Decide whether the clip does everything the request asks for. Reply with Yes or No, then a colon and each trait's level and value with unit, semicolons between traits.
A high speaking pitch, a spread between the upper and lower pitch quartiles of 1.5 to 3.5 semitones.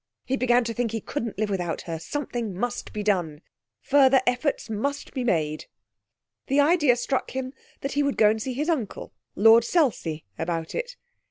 No: high, 240 Hz; average, 5.1 semitones